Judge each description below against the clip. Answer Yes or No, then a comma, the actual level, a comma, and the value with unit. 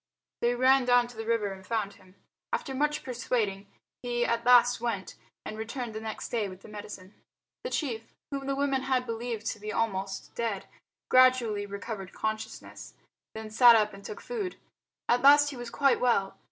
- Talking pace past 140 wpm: Yes, average, 180 wpm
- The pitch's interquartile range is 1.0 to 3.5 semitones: Yes, average, 3.1 semitones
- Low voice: No, high, 230 Hz